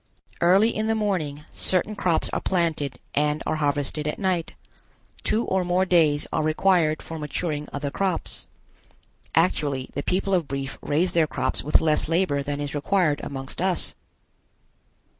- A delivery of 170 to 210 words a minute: No, average, 155 wpm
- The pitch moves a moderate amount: Yes, average, 4.0 semitones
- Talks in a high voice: No, medium, 160 Hz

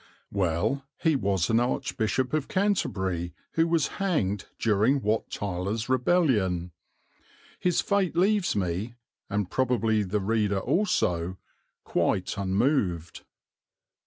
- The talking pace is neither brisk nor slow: No, slow, 105 wpm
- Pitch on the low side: Yes, low, 110 Hz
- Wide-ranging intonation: Yes, wide, 6.9 semitones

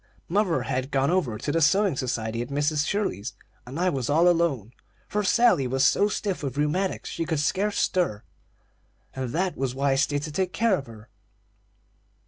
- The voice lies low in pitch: No, medium, 150 Hz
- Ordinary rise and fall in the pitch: No, wide, 5.7 semitones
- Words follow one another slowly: No, average, 185 wpm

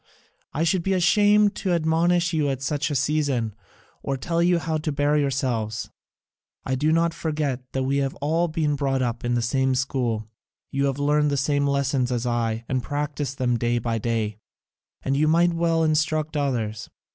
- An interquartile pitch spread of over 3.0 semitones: Yes, average, 3.8 semitones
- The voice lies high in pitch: No, medium, 140 Hz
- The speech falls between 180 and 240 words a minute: Yes, average, 185 wpm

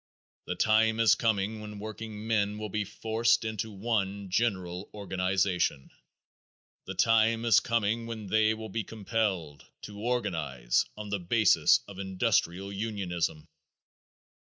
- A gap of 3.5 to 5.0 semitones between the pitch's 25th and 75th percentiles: No, average, 2.8 semitones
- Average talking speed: No, slow, 125 wpm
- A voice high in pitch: No, low, 105 Hz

